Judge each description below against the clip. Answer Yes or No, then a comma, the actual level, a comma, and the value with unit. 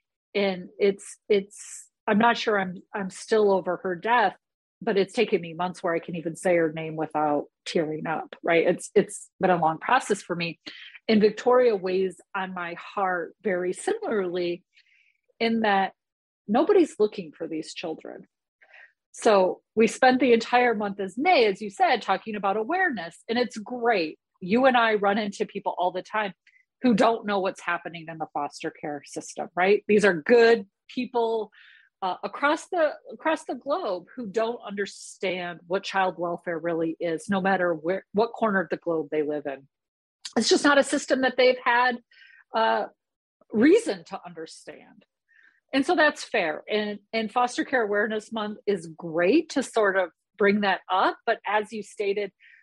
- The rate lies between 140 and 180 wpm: Yes, average, 170 wpm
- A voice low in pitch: No, high, 205 Hz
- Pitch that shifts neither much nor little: Yes, average, 4.7 semitones